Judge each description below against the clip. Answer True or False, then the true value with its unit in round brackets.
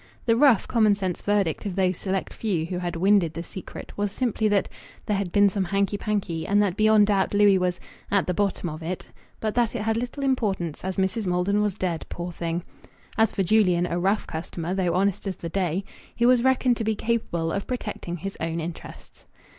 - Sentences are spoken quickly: True (210 wpm)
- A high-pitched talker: True (195 Hz)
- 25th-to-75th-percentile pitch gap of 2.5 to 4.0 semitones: True (3.3 semitones)